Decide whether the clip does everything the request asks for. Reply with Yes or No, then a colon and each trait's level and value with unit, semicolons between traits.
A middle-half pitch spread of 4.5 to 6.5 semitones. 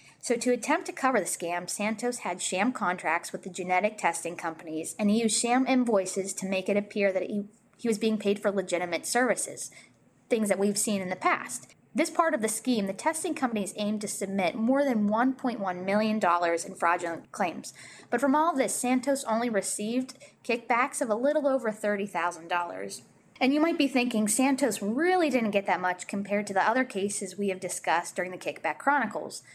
Yes: average, 5.1 semitones